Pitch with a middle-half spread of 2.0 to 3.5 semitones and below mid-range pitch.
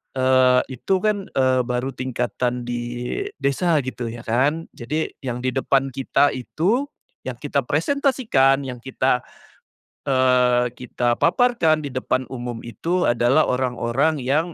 No: average, 3.9 semitones; low, 130 Hz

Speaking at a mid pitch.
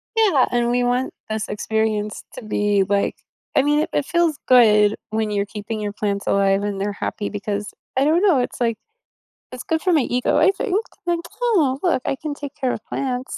No: high, 245 Hz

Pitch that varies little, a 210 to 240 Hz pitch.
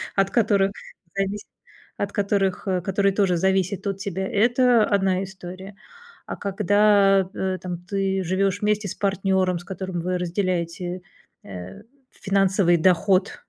No: narrow, 1.5 semitones; high, 190 Hz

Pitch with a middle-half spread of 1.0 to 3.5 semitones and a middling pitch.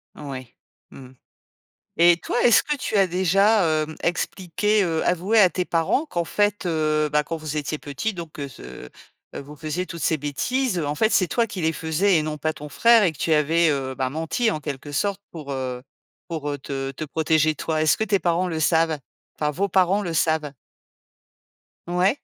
No: average, 3.9 semitones; medium, 160 Hz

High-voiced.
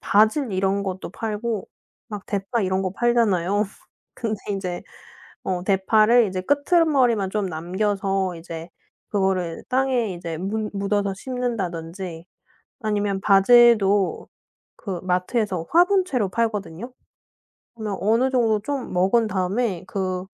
Yes: high, 200 Hz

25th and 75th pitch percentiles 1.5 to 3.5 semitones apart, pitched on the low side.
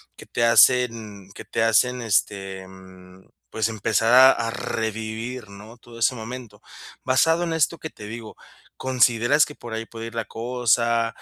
Yes: narrow, 2.4 semitones; low, 115 Hz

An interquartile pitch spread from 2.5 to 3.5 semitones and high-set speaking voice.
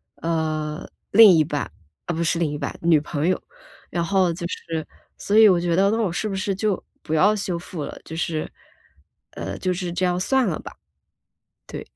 No: average, 3.2 semitones; medium, 175 Hz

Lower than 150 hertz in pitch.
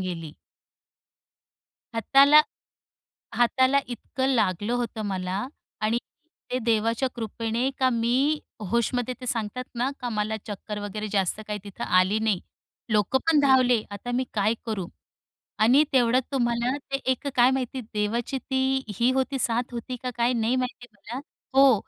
No: high, 235 Hz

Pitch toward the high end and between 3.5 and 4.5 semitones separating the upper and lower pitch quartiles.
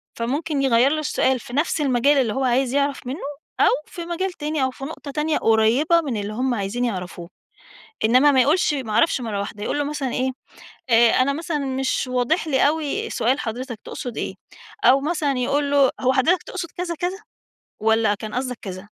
Yes: very high, 265 Hz; average, 3.8 semitones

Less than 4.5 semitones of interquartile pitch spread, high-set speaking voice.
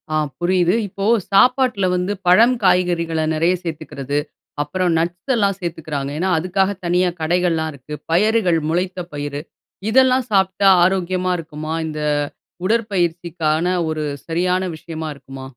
No: average, 3.2 semitones; medium, 175 Hz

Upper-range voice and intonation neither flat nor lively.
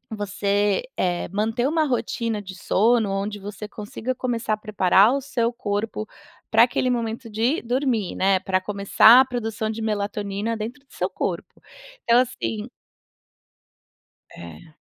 Yes: high, 215 Hz; average, 3.0 semitones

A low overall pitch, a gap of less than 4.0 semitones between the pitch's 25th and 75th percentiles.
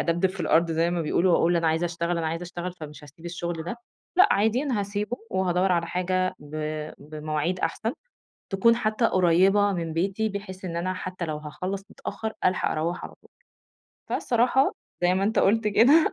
No: medium, 180 Hz; average, 3.3 semitones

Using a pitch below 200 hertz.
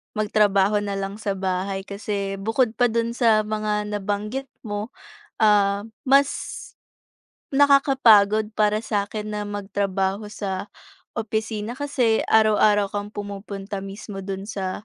No: high, 210 Hz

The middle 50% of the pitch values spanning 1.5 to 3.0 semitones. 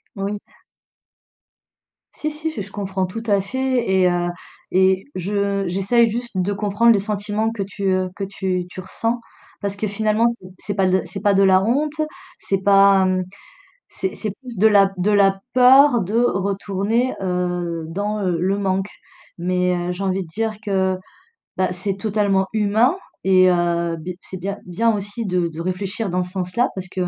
Yes: narrow, 2.4 semitones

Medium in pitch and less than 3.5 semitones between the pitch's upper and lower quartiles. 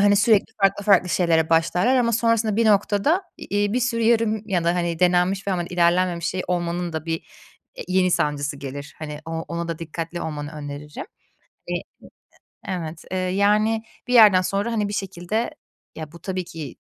No: medium, 180 Hz; average, 3.8 semitones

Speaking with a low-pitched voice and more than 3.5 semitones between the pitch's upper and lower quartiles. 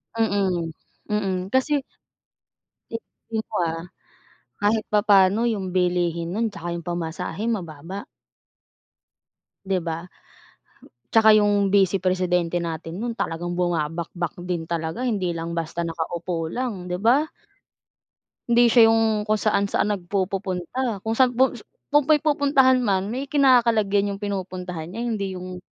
No: high, 195 Hz; average, 4.3 semitones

